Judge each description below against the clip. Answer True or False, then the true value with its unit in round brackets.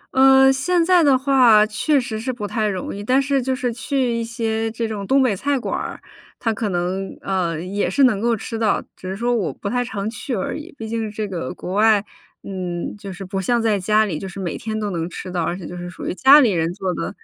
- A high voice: True (215 Hz)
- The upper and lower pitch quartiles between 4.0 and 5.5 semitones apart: True (4.5 semitones)